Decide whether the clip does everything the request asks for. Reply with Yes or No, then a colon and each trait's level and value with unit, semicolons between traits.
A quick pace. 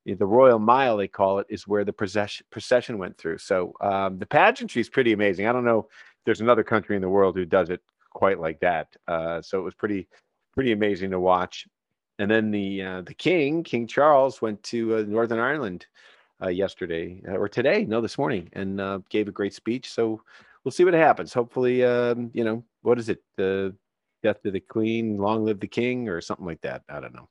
Yes: fast, 215 wpm